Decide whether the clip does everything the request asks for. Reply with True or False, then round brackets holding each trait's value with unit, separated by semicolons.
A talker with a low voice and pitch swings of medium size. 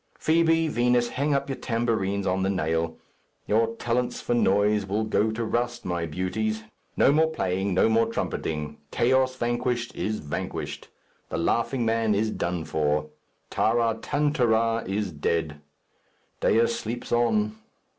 True (110 Hz; 4.1 semitones)